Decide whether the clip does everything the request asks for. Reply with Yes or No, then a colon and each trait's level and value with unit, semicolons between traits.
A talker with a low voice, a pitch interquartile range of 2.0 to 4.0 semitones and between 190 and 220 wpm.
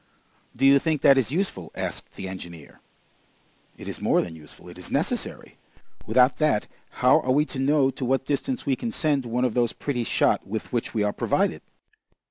No: low, 130 Hz; average, 4.4 semitones; average, 195 wpm